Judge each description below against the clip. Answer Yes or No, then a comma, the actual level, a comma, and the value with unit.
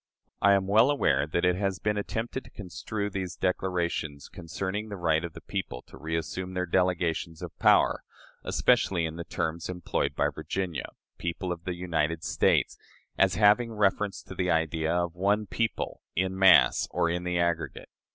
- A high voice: No, very low, 90 Hz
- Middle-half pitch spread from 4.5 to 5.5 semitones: No, average, 3.0 semitones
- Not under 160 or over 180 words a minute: Yes, average, 170 wpm